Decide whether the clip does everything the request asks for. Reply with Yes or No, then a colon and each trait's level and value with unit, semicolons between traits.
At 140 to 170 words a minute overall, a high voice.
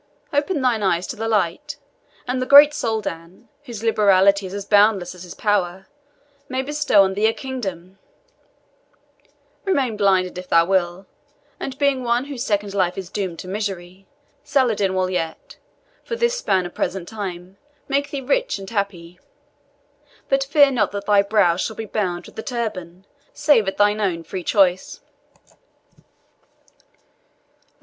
Yes: average, 155 wpm; high, 205 Hz